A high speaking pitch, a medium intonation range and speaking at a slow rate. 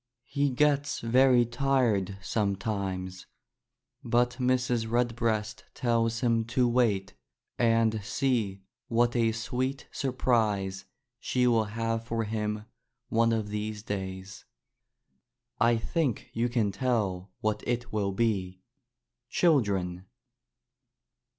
No: low, 115 Hz; average, 3.0 semitones; slow, 105 wpm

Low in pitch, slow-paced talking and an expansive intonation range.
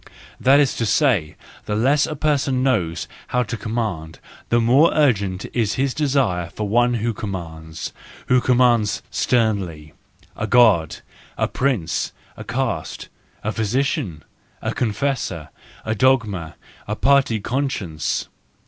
Yes: low, 115 Hz; slow, 125 wpm; wide, 6.0 semitones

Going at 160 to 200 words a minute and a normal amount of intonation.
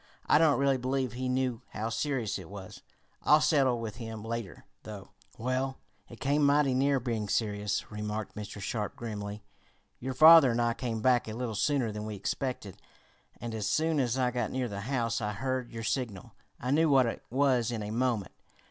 Yes: average, 190 wpm; average, 3.6 semitones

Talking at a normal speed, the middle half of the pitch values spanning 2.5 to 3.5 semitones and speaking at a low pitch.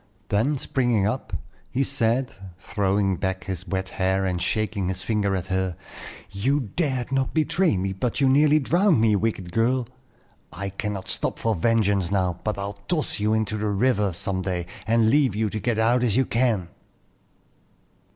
No: average, 170 wpm; average, 4.5 semitones; low, 105 Hz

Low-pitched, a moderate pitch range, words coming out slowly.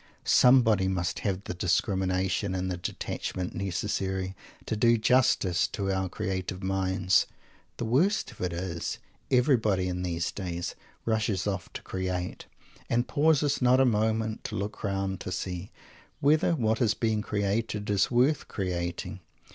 No: low, 100 Hz; average, 3.5 semitones; average, 145 wpm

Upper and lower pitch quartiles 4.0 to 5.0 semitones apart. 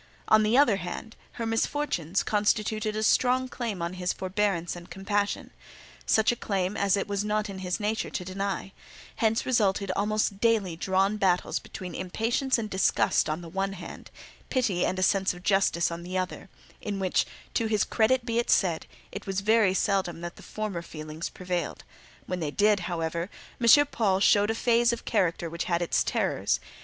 No: average, 3.2 semitones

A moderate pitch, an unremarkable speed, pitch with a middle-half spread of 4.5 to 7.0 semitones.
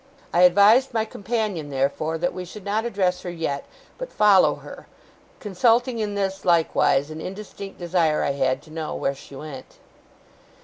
Yes: medium, 180 Hz; average, 165 wpm; average, 5.1 semitones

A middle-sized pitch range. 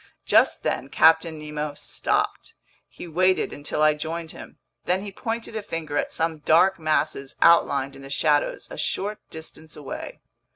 No: narrow, 2.2 semitones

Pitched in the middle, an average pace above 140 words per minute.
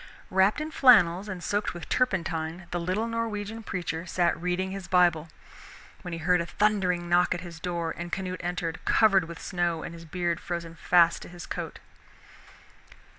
Yes: medium, 175 Hz; average, 175 wpm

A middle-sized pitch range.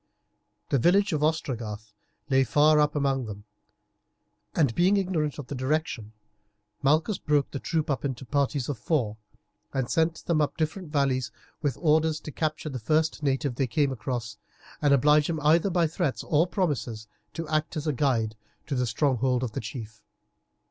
Yes: average, 3.7 semitones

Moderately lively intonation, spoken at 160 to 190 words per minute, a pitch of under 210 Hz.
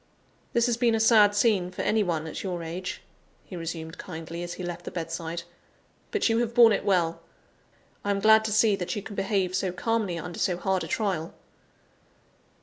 No: average, 4.0 semitones; average, 200 wpm; high, 190 Hz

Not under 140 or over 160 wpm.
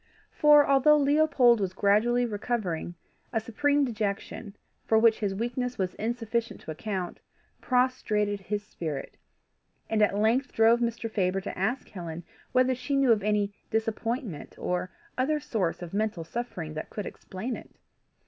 Yes: average, 150 wpm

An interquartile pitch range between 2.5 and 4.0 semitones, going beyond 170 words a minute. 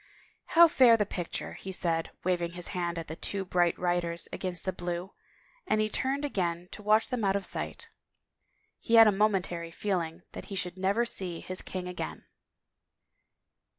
Yes: average, 3.3 semitones; average, 180 wpm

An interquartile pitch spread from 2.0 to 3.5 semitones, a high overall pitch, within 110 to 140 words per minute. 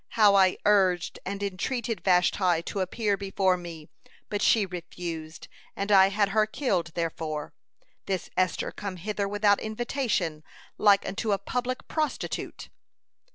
Yes: average, 2.9 semitones; high, 195 Hz; slow, 135 wpm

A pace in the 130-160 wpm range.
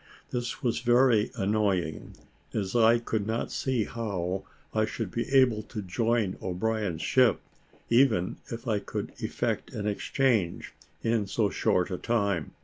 Yes: average, 140 wpm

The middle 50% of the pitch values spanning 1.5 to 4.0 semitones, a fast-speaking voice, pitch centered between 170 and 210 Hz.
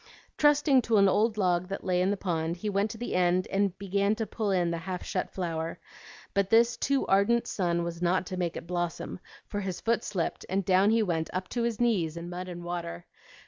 Yes: average, 3.3 semitones; fast, 225 wpm; medium, 185 Hz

